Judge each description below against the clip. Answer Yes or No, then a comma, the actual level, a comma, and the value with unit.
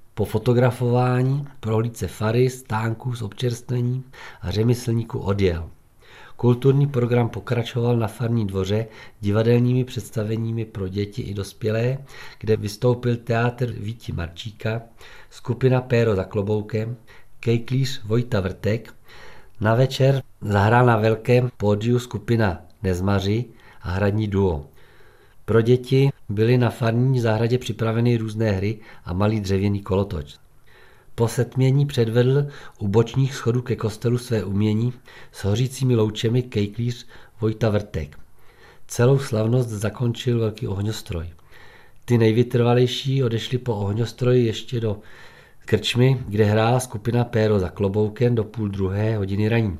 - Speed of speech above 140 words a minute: No, average, 120 wpm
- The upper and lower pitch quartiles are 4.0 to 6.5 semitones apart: No, average, 2.7 semitones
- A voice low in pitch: Yes, low, 115 Hz